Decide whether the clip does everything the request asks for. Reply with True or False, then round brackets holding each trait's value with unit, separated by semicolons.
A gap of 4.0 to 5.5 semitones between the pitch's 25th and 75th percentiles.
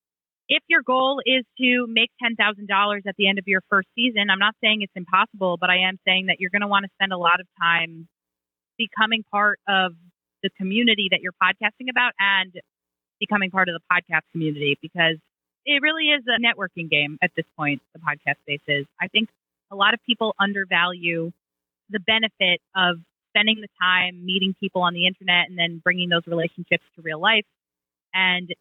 False (3.6 semitones)